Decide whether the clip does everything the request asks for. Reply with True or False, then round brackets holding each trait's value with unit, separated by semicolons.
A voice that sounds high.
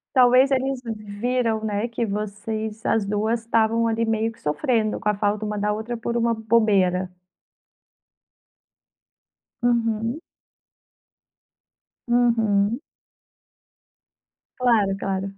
True (220 Hz)